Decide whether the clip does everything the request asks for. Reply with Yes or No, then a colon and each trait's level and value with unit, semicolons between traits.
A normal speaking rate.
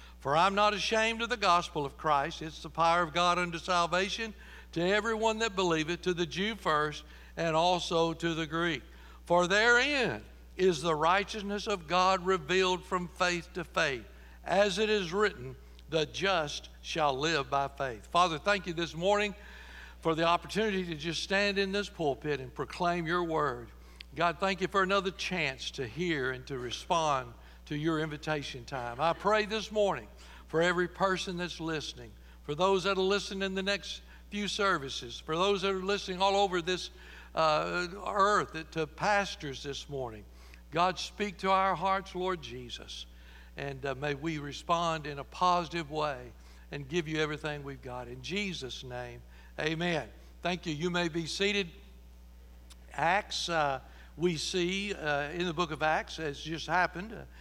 Yes: average, 170 wpm